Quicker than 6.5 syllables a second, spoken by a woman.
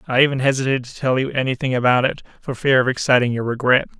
No: 7.0 syllables/s; male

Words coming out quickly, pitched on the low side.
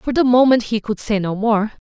No: fast, 255 wpm; high, 225 Hz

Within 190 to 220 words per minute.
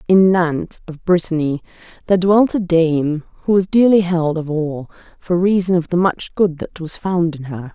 Yes: average, 195 wpm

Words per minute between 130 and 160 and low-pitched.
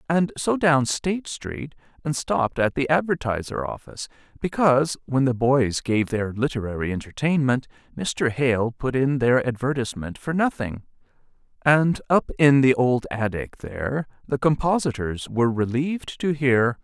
Yes: average, 145 wpm; low, 130 Hz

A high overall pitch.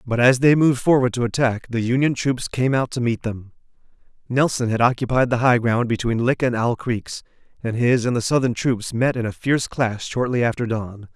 No: low, 120 Hz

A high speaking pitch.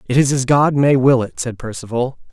No: low, 130 Hz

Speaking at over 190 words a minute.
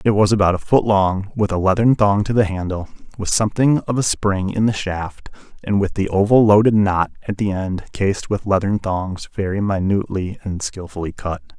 Yes: average, 200 wpm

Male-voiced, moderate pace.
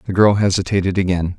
Yes: male; average, 175 wpm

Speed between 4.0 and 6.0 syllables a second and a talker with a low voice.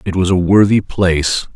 Yes: 5.0 syllables/s; very low, 90 Hz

